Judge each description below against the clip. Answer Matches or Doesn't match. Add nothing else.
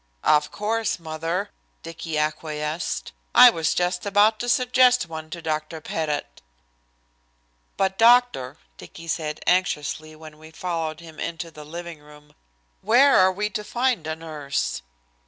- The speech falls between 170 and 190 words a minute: Doesn't match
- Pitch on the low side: Doesn't match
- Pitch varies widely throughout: Doesn't match